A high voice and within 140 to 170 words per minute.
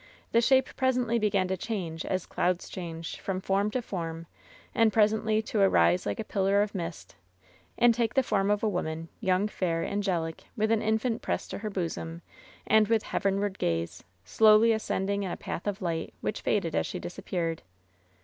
No: high, 200 Hz; average, 180 wpm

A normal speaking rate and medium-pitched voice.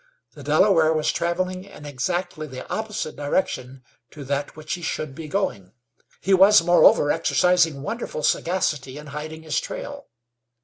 Yes: average, 145 wpm; medium, 155 Hz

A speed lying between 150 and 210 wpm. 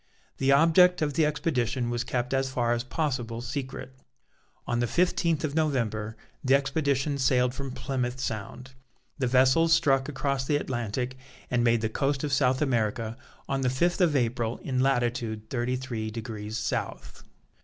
Yes: average, 160 wpm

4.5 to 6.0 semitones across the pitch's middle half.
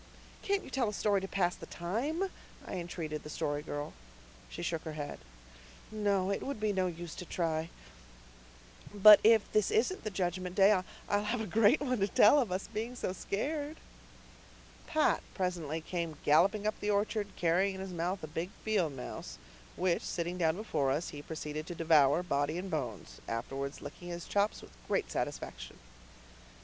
Yes: average, 4.8 semitones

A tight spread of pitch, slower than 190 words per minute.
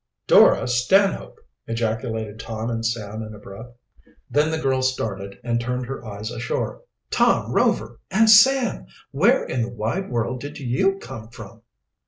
No: average, 3.4 semitones; average, 155 wpm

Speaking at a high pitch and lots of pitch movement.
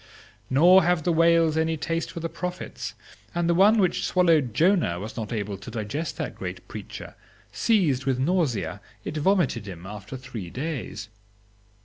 No: medium, 155 Hz; wide, 7.6 semitones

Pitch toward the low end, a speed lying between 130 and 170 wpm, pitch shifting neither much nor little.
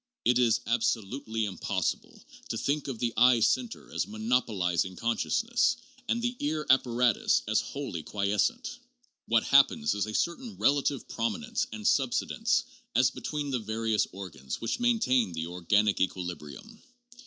No: low, 115 Hz; average, 140 wpm; wide, 5.7 semitones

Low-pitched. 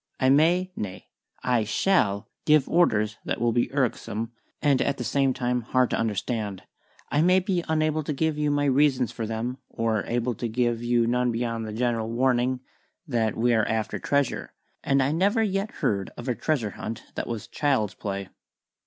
Yes: low, 125 Hz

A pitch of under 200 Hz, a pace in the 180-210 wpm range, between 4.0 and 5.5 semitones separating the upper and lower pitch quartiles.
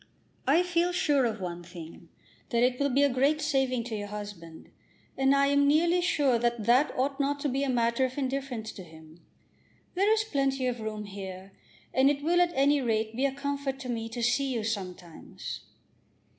No: very high, 255 Hz; average, 200 wpm; average, 4.5 semitones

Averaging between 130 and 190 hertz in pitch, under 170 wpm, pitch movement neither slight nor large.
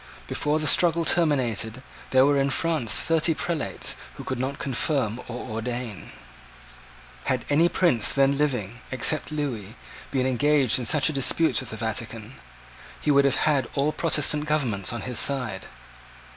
Yes: low, 135 Hz; average, 155 wpm; average, 4.1 semitones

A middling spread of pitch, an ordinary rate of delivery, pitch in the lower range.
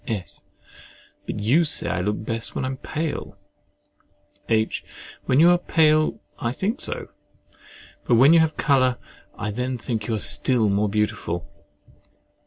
No: wide, 6.1 semitones; average, 155 wpm; low, 125 Hz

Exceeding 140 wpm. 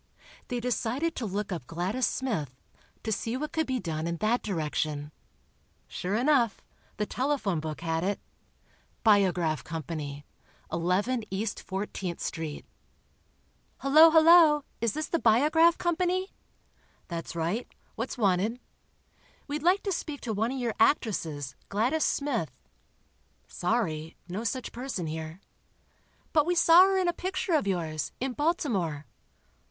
No: slow, 135 wpm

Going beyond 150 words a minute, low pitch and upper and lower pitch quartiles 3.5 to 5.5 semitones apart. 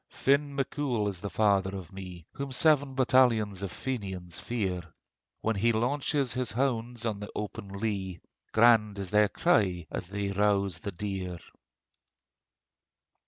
No: average, 145 wpm; low, 105 Hz; average, 4.2 semitones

